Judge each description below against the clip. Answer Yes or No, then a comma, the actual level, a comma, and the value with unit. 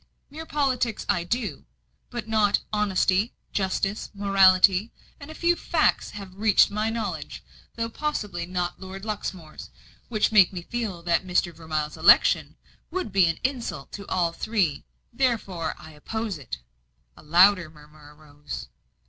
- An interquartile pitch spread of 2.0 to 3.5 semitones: No, average, 4.7 semitones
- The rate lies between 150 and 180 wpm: No, average, 140 wpm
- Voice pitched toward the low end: No, high, 195 Hz